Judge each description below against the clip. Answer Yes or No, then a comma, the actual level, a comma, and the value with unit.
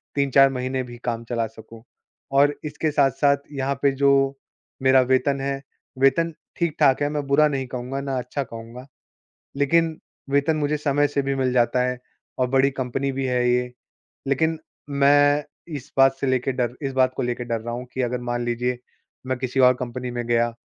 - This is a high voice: No, low, 135 Hz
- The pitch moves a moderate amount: No, narrow, 2.2 semitones